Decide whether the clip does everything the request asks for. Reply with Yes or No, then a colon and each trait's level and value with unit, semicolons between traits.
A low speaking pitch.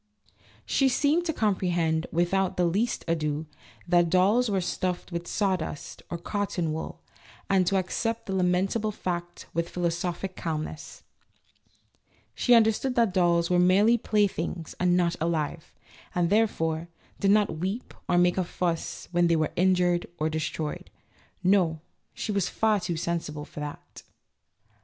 No: medium, 180 Hz